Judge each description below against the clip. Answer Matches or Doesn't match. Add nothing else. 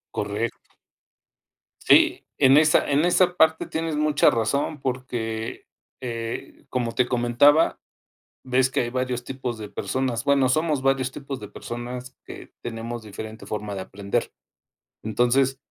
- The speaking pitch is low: Matches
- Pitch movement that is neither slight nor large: Matches